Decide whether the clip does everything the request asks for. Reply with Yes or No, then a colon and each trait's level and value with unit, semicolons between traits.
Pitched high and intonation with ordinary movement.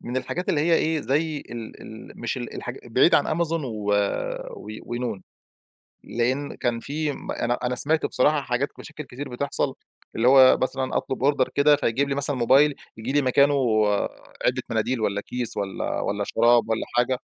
No: low, 130 Hz; average, 3.3 semitones